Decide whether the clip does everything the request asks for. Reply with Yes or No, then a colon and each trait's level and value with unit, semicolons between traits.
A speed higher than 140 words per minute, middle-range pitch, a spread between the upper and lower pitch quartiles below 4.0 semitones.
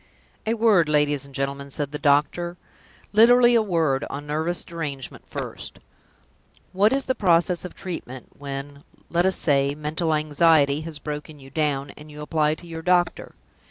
Yes: average, 160 wpm; medium, 155 Hz; average, 3.5 semitones